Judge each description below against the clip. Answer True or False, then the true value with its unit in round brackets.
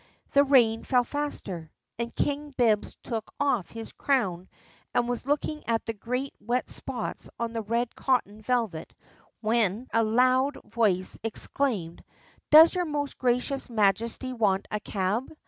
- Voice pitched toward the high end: True (235 Hz)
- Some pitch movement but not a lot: True (3.7 semitones)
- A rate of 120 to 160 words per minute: True (145 wpm)